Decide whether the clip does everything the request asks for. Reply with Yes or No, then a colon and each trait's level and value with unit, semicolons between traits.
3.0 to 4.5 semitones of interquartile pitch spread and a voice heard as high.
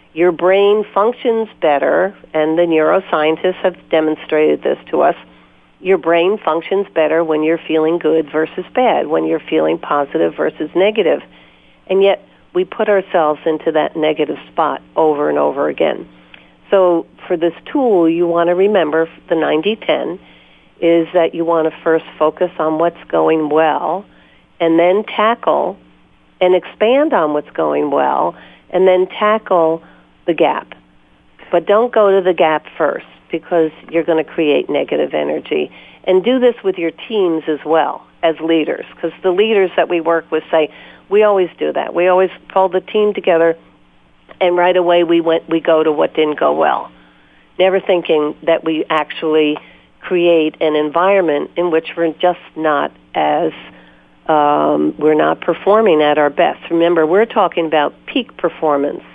No: average, 3.3 semitones; medium, 165 Hz